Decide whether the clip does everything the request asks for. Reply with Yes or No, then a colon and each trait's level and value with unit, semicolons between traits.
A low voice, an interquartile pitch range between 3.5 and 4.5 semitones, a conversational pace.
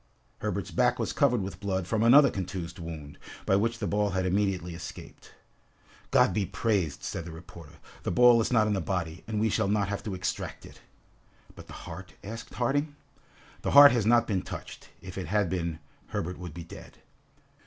Yes: very low, 95 Hz; average, 3.9 semitones; average, 195 wpm